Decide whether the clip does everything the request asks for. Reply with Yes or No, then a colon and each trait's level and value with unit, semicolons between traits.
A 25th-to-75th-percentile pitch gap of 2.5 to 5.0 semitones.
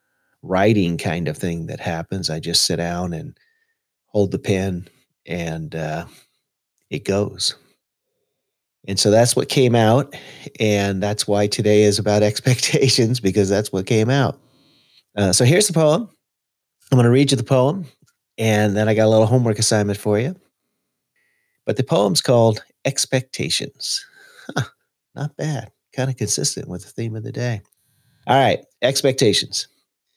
No: wide, 5.4 semitones